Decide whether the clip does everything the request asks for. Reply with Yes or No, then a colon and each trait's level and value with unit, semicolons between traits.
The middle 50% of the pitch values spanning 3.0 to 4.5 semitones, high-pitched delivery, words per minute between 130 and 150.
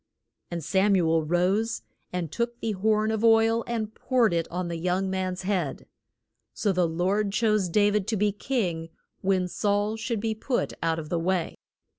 No: average, 3.7 semitones; high, 195 Hz; average, 185 wpm